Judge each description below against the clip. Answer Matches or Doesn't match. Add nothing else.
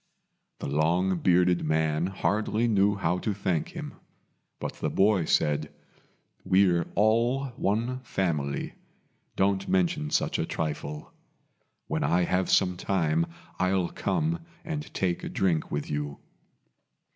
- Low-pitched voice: Matches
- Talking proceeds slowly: Matches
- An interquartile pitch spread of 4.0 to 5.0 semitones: Matches